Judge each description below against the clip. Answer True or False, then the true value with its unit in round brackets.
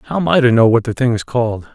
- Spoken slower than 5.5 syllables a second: False (5.9 syllables/s)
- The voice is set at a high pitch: False (120 Hz)